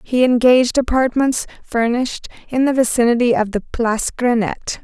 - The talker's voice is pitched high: Yes, high, 240 Hz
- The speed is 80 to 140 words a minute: Yes, slow, 135 wpm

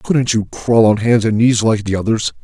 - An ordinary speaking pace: No, fast, 245 wpm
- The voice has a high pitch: No, low, 110 Hz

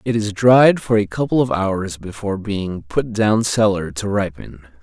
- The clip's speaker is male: Yes, male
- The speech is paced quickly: No, average, 185 wpm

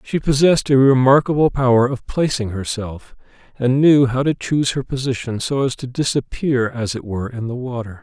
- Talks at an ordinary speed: Yes, average, 185 wpm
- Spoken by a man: Yes, male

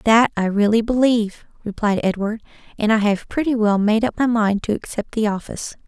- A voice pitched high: Yes, high, 220 Hz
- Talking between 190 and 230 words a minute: Yes, average, 195 wpm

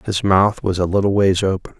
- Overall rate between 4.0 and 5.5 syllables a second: Yes, 5.4 syllables/s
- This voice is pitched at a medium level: No, very low, 95 Hz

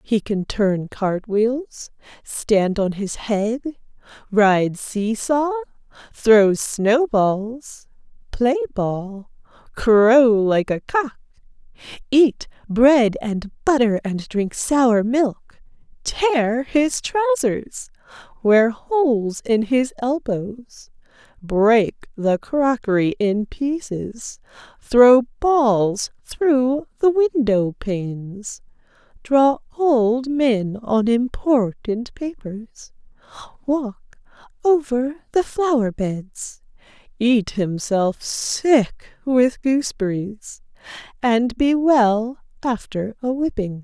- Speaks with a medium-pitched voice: No, high, 240 Hz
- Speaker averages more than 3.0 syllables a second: No, 2.8 syllables/s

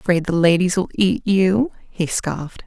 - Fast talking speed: No, average, 180 wpm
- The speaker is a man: No, female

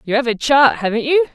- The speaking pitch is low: No, very high, 255 Hz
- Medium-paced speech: No, fast, 265 wpm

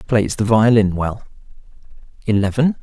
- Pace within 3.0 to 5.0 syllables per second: Yes, 4.9 syllables/s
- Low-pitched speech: Yes, low, 110 Hz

